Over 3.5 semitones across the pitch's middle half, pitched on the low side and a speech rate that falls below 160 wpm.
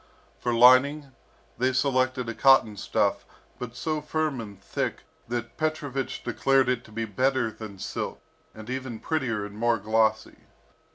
No: average, 3.2 semitones; low, 125 Hz; average, 150 wpm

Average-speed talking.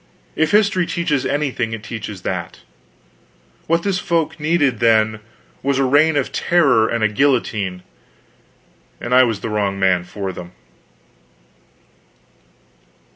No: slow, 130 wpm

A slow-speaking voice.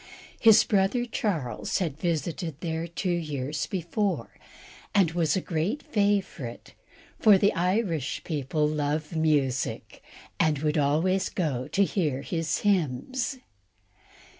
Yes: slow, 115 wpm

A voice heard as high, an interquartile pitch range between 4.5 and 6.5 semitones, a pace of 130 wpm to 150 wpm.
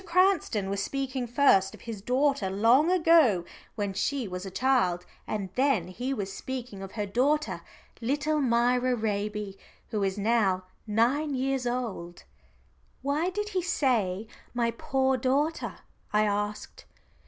Yes: high, 240 Hz; average, 5.3 semitones; average, 140 wpm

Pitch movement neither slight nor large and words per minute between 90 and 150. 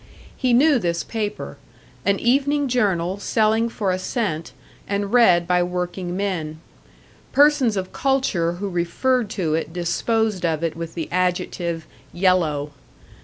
Yes: average, 4.9 semitones; slow, 135 wpm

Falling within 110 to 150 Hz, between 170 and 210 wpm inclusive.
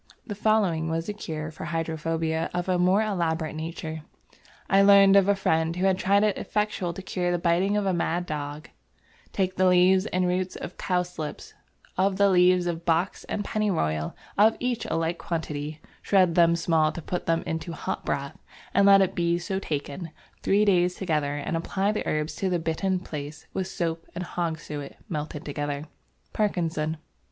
No: medium, 175 Hz; average, 180 wpm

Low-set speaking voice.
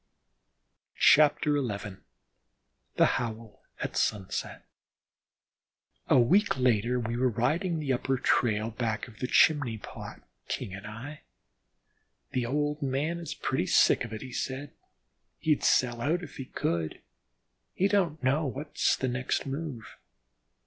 Yes: low, 130 Hz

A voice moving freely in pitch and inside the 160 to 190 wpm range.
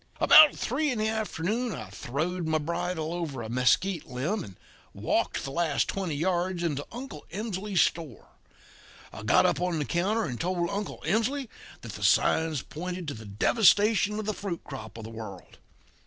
Yes: wide, 6.1 semitones; average, 180 wpm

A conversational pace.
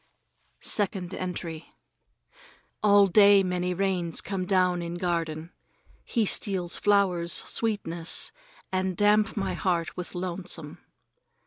No: slow, 105 wpm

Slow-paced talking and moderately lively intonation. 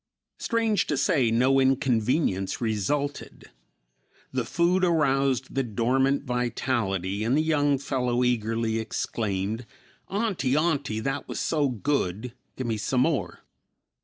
Yes: slow, 120 wpm; average, 4.1 semitones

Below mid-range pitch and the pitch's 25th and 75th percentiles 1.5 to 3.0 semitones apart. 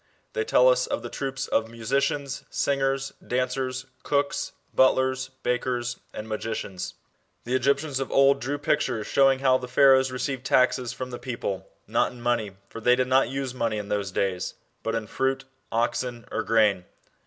Yes: low, 130 Hz; average, 2.7 semitones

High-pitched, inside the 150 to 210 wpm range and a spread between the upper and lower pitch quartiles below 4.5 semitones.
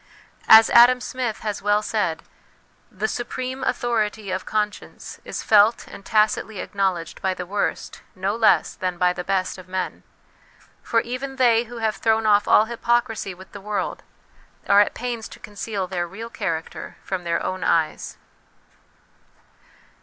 Yes: high, 210 Hz; average, 155 wpm; average, 3.4 semitones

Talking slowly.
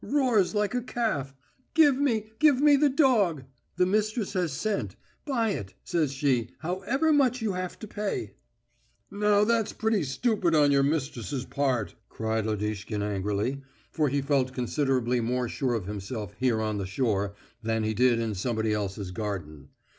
No: average, 160 wpm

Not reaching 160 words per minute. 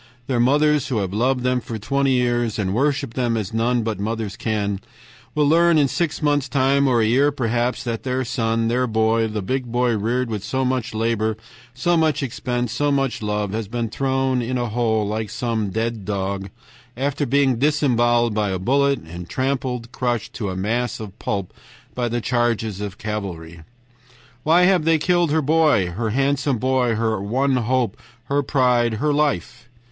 No: average, 180 wpm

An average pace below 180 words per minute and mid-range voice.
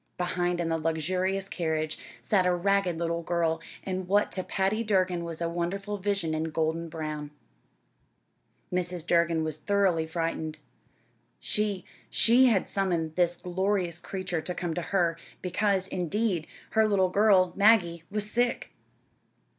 Yes: average, 140 wpm; medium, 180 Hz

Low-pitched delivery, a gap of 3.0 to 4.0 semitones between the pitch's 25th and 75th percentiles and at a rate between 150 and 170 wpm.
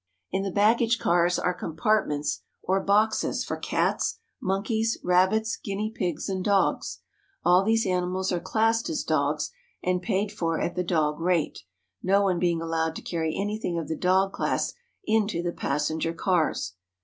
No: medium, 185 Hz; average, 3.7 semitones; average, 160 wpm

